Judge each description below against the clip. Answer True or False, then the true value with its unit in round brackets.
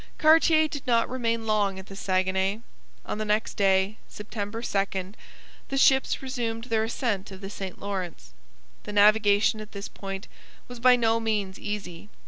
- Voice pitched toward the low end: False (210 Hz)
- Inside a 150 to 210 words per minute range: True (160 wpm)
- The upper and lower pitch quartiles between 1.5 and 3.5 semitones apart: True (2.9 semitones)